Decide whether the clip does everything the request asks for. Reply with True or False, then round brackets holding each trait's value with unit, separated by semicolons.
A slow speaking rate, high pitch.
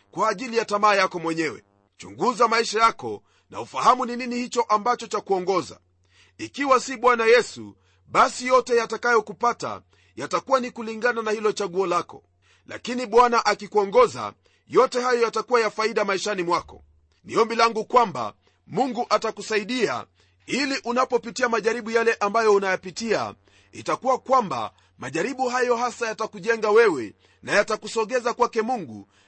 False (125 wpm; 230 Hz)